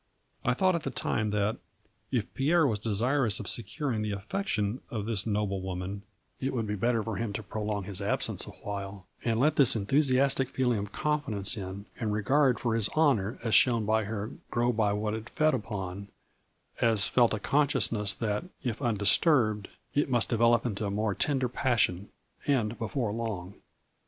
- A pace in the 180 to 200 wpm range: Yes, average, 185 wpm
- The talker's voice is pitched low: Yes, low, 110 Hz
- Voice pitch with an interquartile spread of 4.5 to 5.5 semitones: No, average, 3.7 semitones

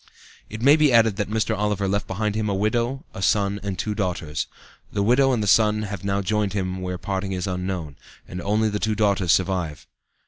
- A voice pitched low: Yes, low, 100 Hz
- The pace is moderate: No, fast, 210 wpm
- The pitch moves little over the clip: Yes, narrow, 2.3 semitones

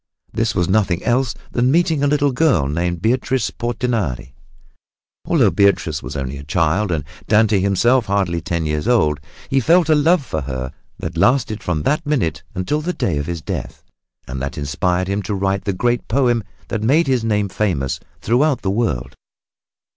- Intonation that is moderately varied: No, wide, 7.2 semitones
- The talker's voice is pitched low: Yes, low, 100 Hz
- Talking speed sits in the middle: Yes, average, 175 wpm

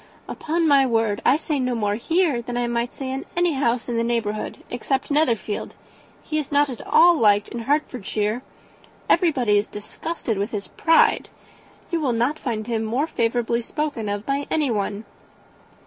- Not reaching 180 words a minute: Yes, average, 170 wpm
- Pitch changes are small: No, average, 4.7 semitones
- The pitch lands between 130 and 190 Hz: No, high, 240 Hz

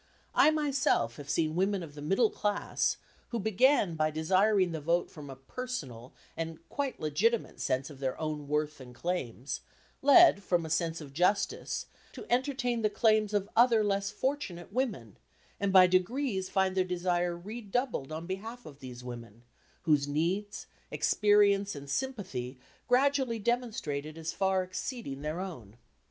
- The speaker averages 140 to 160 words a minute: Yes, average, 155 wpm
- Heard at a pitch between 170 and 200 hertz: Yes, medium, 185 Hz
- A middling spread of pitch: No, wide, 6.4 semitones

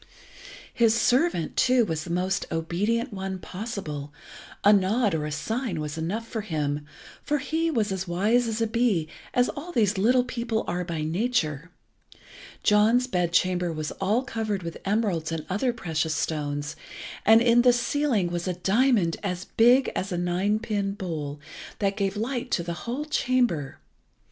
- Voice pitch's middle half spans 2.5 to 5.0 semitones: No, wide, 5.6 semitones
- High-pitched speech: Yes, high, 200 Hz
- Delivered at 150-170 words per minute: Yes, average, 165 wpm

